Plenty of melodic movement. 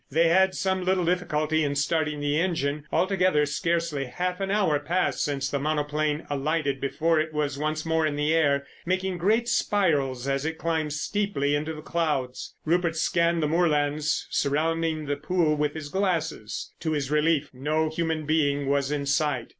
No: narrow, 2.5 semitones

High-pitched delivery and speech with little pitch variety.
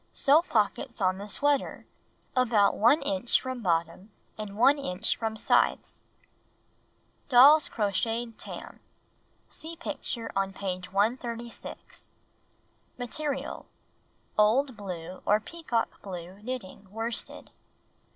No: high, 225 Hz; average, 4.8 semitones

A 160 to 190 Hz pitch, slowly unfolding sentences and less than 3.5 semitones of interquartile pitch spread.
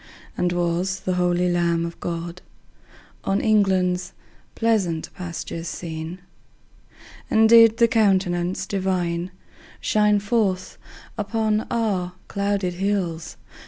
Yes: medium, 185 Hz; slow, 100 wpm; average, 2.9 semitones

